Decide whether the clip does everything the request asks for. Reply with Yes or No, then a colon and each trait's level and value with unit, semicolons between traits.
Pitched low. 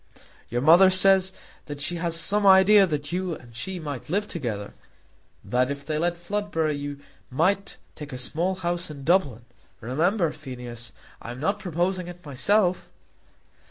No: medium, 165 Hz